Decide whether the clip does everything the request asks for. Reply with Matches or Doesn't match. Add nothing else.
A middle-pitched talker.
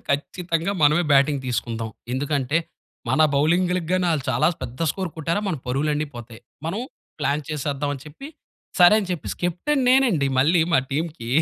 Matches